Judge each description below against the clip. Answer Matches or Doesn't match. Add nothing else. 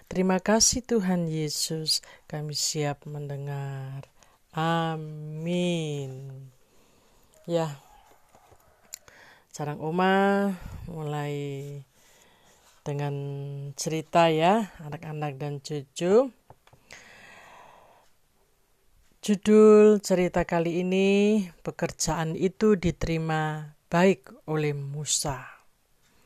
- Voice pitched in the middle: Matches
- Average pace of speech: Doesn't match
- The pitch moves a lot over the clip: Doesn't match